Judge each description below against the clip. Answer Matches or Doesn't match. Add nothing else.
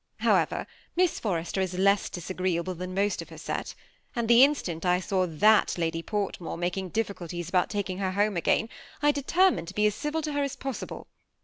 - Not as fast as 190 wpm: Doesn't match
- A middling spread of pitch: Matches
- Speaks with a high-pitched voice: Matches